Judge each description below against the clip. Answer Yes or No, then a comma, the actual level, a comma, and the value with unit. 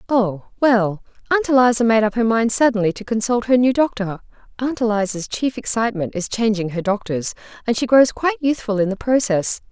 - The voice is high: Yes, high, 225 Hz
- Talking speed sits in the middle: Yes, average, 180 wpm